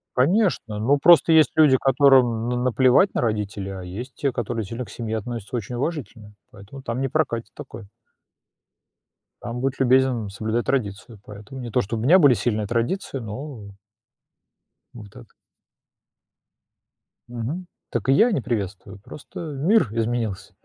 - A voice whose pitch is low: Yes, low, 120 Hz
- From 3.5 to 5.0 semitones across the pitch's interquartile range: Yes, average, 3.9 semitones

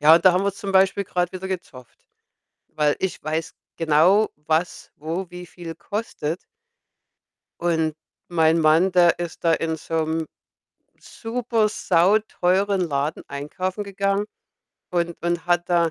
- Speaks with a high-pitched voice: No, medium, 175 Hz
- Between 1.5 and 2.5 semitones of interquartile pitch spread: No, average, 2.9 semitones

